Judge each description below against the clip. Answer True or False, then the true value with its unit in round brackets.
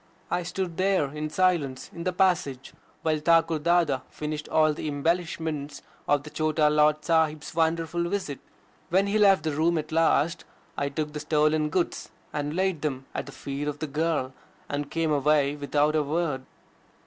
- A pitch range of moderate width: False (2.2 semitones)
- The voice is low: False (155 Hz)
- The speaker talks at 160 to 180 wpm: True (170 wpm)